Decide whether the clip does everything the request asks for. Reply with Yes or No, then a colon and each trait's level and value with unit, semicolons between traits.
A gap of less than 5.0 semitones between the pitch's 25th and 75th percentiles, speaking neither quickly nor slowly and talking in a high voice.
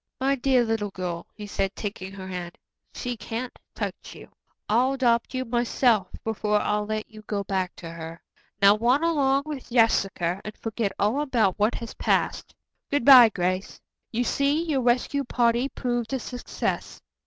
Yes: average, 4.3 semitones; average, 165 wpm; high, 230 Hz